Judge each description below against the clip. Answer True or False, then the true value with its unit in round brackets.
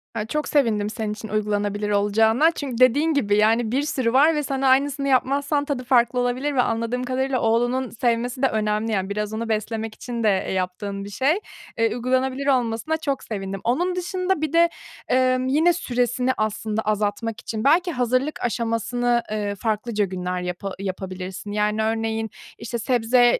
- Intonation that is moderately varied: True (3.7 semitones)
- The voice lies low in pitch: False (235 Hz)